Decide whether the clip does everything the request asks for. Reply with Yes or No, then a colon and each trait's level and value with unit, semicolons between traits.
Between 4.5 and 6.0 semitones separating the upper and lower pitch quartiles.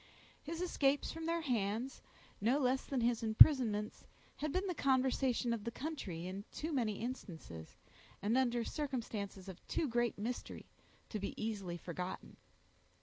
Yes: average, 4.9 semitones